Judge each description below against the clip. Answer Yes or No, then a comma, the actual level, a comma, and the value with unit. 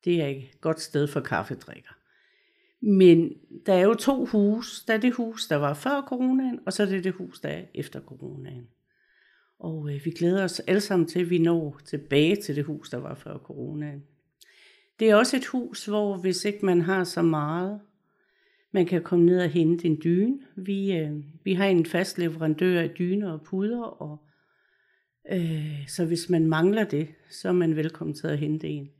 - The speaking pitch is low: No, medium, 175 Hz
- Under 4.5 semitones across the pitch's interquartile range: No, average, 4.9 semitones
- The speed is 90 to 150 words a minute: No, average, 200 wpm